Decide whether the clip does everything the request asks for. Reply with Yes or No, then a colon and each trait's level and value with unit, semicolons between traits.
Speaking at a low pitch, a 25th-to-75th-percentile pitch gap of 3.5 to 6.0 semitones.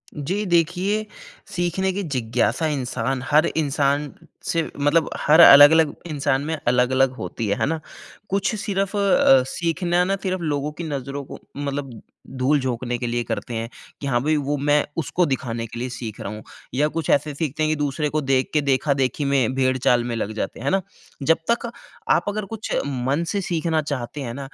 No: medium, 145 Hz; average, 4.2 semitones